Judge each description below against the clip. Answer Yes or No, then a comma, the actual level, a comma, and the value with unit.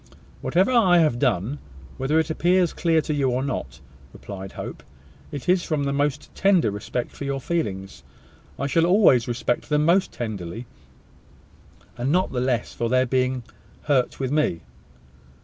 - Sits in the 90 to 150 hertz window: Yes, medium, 140 Hz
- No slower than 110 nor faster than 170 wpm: Yes, average, 160 wpm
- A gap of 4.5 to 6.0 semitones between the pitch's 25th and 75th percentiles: Yes, average, 4.9 semitones